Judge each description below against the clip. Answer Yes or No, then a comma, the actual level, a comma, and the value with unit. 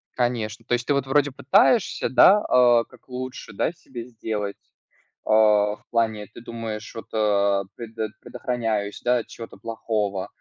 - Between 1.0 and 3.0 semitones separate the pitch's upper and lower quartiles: Yes, average, 2.7 semitones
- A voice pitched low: Yes, low, 115 Hz